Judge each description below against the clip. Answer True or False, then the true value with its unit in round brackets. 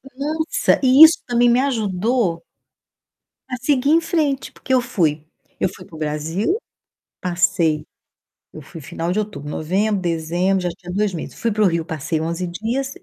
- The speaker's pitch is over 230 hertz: False (190 Hz)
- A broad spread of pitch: True (7.1 semitones)